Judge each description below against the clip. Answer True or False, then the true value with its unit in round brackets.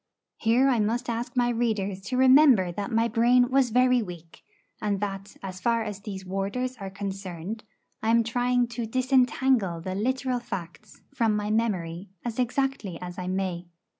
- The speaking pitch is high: True (220 Hz)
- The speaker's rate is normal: True (165 wpm)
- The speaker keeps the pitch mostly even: False (4.3 semitones)